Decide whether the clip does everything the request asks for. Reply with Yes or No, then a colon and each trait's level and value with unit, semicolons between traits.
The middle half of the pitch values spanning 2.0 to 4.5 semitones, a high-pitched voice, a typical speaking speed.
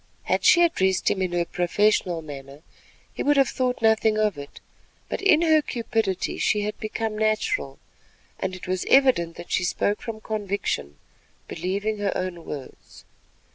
Yes: average, 4.1 semitones; high, 205 Hz; average, 160 wpm